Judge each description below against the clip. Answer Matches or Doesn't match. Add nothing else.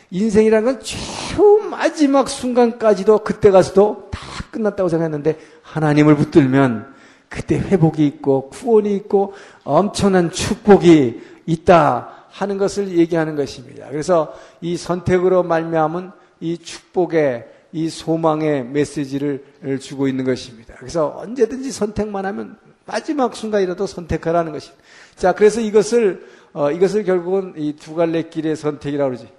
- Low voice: Doesn't match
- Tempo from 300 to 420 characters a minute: Matches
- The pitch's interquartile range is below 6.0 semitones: Matches